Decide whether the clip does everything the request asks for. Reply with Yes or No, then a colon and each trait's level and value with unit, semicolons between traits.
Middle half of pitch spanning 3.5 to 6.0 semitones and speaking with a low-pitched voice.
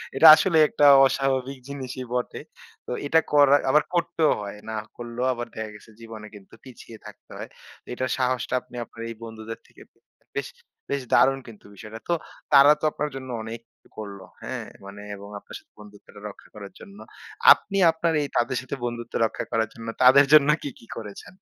Yes: average, 4.0 semitones; low, 125 Hz